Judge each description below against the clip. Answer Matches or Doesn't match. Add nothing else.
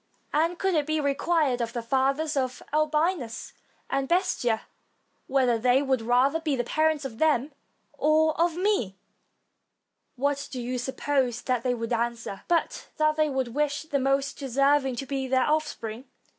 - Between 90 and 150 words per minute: Doesn't match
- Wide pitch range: Doesn't match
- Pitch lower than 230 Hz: Doesn't match